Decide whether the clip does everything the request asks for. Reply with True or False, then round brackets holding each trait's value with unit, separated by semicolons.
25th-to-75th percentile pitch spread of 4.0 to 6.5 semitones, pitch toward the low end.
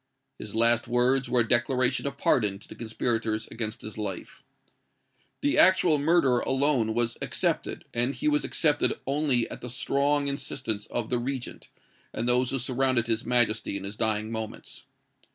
False (3.4 semitones; 120 Hz)